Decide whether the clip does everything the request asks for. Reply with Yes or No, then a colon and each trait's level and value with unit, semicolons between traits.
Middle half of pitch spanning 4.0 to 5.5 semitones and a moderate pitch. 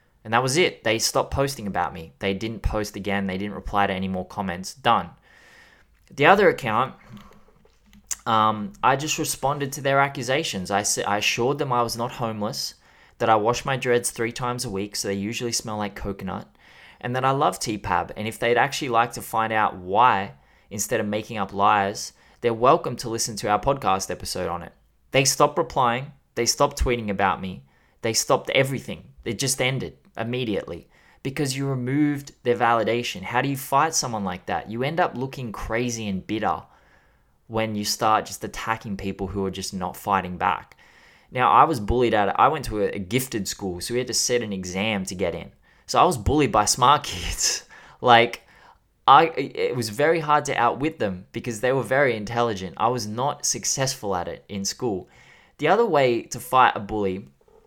No: average, 4.7 semitones; low, 115 Hz